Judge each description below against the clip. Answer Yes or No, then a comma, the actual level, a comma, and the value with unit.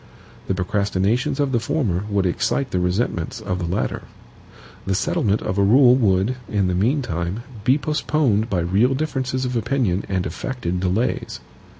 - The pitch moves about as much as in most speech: No, wide, 5.7 semitones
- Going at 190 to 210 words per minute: No, average, 160 wpm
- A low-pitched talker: Yes, low, 105 Hz